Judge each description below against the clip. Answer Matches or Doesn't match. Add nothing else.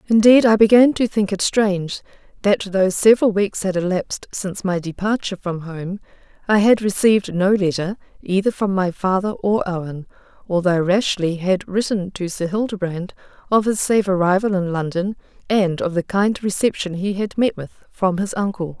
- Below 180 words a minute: Matches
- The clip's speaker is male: Doesn't match